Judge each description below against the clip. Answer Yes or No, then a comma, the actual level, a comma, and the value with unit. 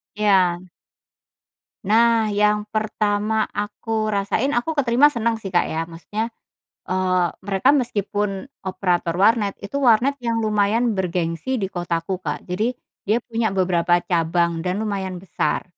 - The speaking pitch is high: Yes, high, 205 Hz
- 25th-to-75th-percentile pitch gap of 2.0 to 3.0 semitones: No, average, 3.7 semitones